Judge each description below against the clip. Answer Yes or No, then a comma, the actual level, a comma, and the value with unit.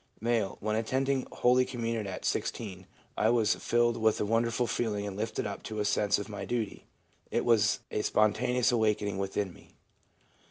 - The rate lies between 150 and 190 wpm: Yes, average, 170 wpm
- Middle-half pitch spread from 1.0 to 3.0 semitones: Yes, narrow, 2.4 semitones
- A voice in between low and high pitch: No, low, 110 Hz